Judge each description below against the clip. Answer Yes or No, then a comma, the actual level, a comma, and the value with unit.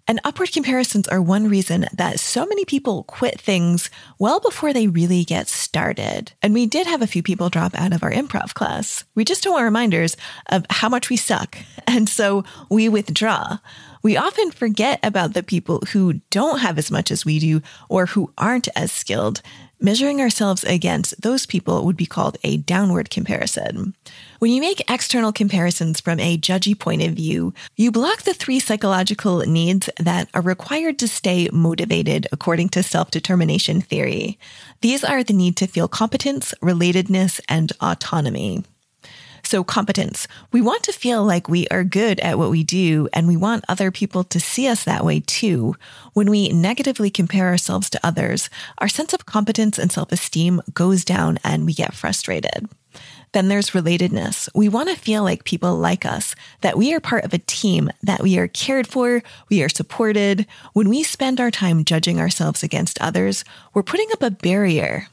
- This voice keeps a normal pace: Yes, average, 180 wpm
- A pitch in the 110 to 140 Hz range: No, high, 195 Hz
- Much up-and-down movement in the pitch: No, average, 4.7 semitones